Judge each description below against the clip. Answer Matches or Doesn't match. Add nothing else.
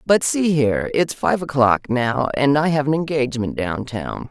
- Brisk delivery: Doesn't match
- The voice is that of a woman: Matches